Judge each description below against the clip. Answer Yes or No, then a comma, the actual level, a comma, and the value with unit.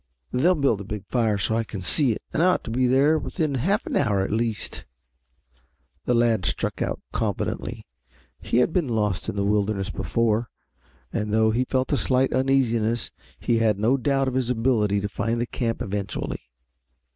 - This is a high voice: No, low, 115 Hz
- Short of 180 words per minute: No, average, 190 wpm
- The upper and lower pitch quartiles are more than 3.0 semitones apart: Yes, average, 3.6 semitones